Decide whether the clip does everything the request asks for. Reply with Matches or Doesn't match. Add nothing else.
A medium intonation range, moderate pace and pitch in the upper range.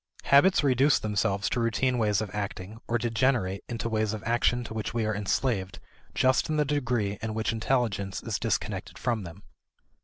Doesn't match